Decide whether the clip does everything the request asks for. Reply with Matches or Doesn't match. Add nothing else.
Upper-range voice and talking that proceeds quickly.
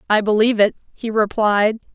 Doesn't match